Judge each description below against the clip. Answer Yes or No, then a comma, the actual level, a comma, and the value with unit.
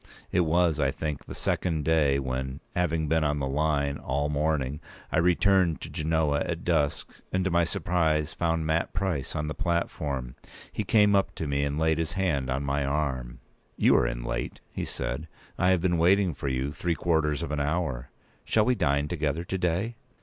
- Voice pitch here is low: Yes, very low, 80 Hz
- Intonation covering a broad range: No, average, 3.4 semitones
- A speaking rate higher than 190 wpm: Yes, average, 200 wpm